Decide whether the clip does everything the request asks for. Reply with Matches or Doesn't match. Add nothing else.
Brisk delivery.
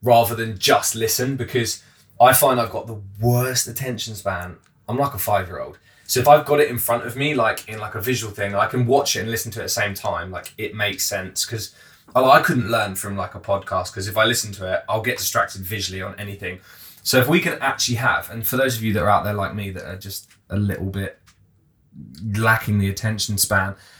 Matches